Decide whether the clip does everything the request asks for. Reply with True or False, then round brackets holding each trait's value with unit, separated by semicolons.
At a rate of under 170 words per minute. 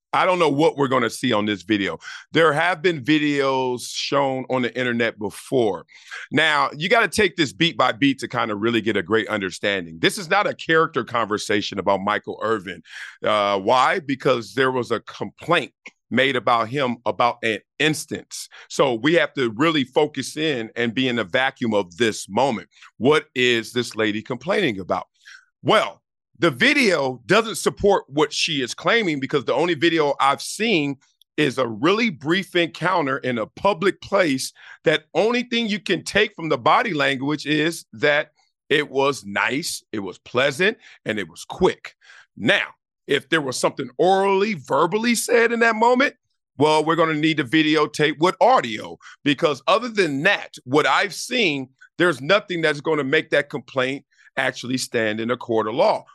False (180 wpm)